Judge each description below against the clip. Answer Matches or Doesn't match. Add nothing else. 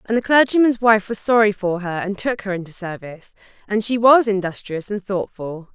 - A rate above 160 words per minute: Matches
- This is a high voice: Matches